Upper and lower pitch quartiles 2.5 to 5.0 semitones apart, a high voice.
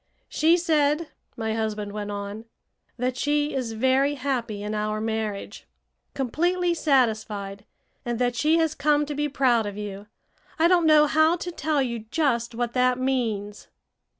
No: wide, 5.5 semitones; very high, 250 Hz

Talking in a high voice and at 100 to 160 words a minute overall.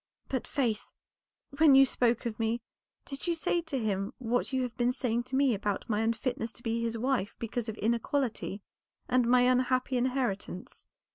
No: high, 240 Hz; average, 180 wpm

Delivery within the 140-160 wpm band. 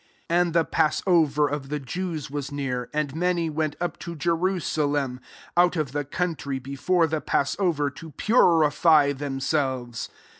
Yes: average, 145 wpm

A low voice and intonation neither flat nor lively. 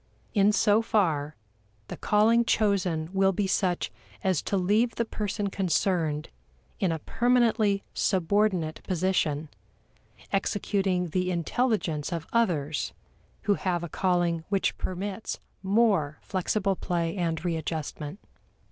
No: medium, 185 Hz; average, 3.7 semitones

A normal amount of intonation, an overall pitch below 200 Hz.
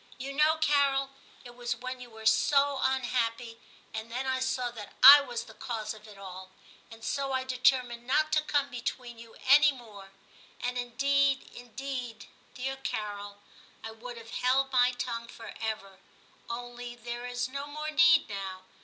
No: average, 3.0 semitones; high, 245 Hz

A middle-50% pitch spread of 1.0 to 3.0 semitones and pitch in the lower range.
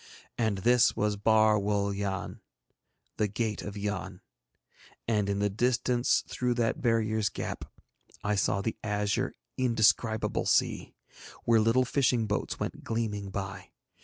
Yes: narrow, 2.4 semitones; low, 110 Hz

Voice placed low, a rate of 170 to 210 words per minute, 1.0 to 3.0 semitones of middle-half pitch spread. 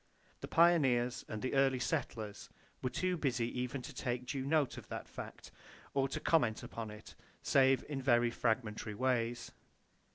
No: low, 125 Hz; average, 160 wpm; narrow, 2.5 semitones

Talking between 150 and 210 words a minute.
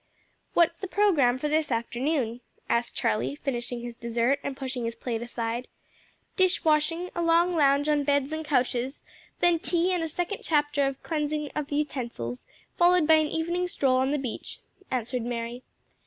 Yes: average, 170 wpm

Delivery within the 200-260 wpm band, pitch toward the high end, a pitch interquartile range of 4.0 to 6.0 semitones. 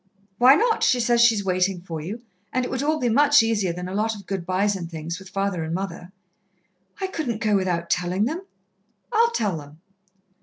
Yes: fast, 205 wpm; high, 200 Hz; average, 5.2 semitones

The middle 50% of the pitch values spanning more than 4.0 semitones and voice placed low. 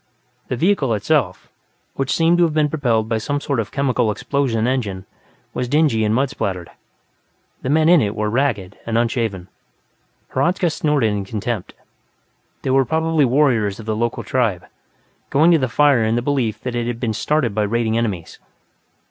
Yes: average, 4.6 semitones; low, 120 Hz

